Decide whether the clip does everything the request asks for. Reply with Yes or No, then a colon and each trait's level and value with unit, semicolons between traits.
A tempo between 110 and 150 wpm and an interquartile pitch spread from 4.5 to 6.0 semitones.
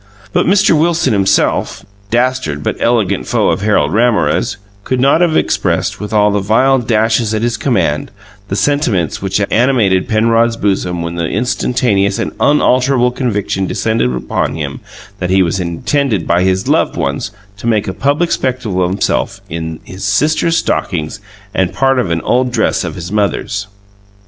No: average, 165 wpm; average, 5.1 semitones